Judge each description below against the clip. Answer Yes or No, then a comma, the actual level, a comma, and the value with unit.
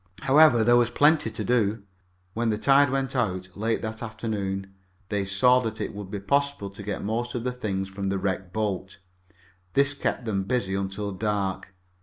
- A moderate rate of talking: Yes, average, 185 wpm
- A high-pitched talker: No, low, 110 Hz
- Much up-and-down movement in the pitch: No, average, 3.9 semitones